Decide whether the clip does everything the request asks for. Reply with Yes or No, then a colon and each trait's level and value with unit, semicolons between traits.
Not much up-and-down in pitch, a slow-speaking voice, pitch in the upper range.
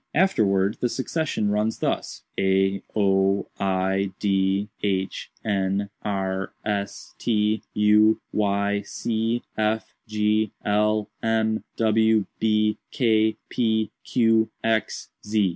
No: narrow, 1.9 semitones; slow, 105 wpm; low, 105 Hz